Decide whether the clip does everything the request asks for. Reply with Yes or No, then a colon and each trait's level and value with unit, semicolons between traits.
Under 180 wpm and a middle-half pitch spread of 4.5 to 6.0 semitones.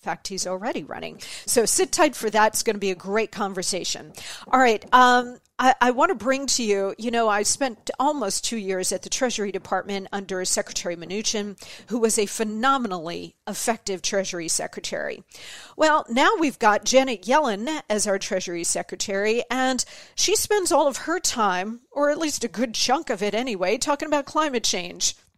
Yes: average, 170 wpm; average, 5.3 semitones